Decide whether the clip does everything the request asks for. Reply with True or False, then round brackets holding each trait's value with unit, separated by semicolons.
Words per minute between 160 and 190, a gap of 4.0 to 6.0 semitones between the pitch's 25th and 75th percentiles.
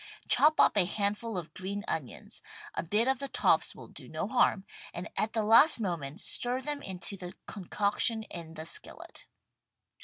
True (175 wpm; 4.4 semitones)